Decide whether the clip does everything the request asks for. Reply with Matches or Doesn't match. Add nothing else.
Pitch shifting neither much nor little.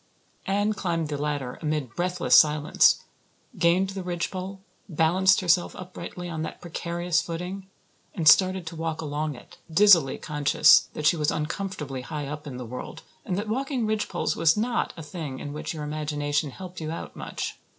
Matches